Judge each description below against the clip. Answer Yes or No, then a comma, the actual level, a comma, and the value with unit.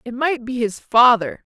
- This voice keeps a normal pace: Yes, average, 190 wpm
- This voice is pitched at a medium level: No, high, 245 Hz